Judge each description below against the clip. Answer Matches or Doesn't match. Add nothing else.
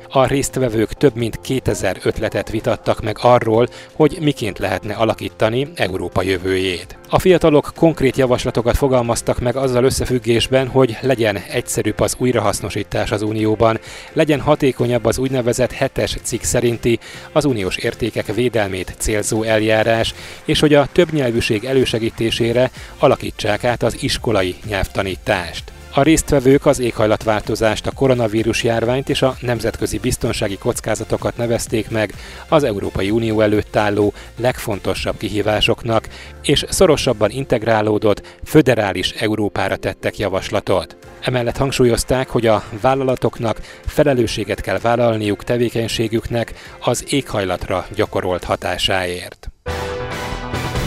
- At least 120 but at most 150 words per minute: Doesn't match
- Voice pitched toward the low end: Matches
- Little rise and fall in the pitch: Doesn't match